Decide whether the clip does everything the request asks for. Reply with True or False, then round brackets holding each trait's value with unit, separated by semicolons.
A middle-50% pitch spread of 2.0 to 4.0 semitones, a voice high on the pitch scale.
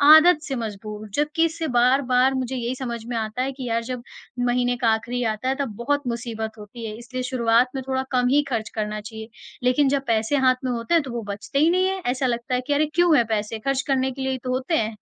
True (2.8 semitones; 250 Hz)